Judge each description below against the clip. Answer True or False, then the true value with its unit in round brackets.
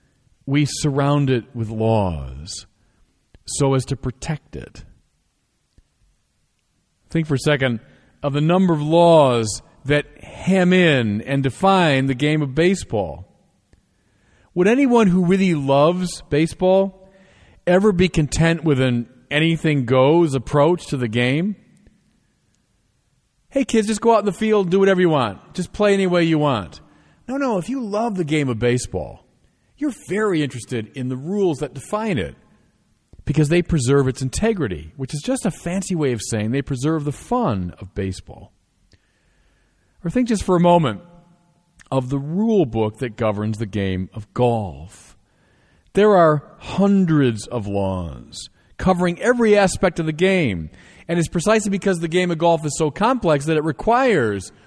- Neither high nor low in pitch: True (150 Hz)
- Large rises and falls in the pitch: True (7.3 semitones)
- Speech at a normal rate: True (155 wpm)